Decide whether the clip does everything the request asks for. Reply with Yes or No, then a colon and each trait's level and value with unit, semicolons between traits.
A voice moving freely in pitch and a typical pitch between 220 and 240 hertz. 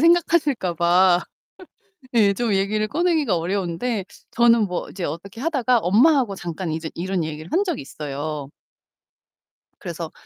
No: wide, 6.5 semitones; high, 195 Hz